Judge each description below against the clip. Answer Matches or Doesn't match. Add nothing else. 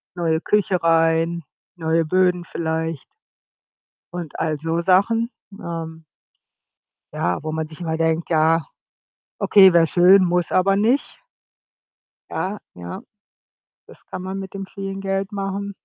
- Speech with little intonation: Doesn't match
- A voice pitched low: Doesn't match